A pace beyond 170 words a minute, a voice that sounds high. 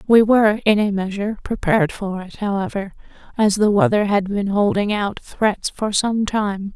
Yes: average, 180 wpm; high, 205 Hz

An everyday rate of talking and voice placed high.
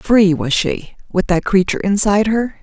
Yes: average, 185 wpm; high, 195 Hz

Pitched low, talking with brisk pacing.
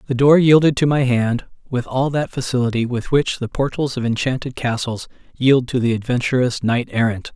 No: low, 125 Hz; average, 190 wpm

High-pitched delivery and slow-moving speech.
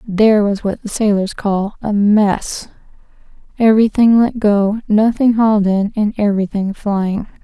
Yes: high, 210 Hz; slow, 130 wpm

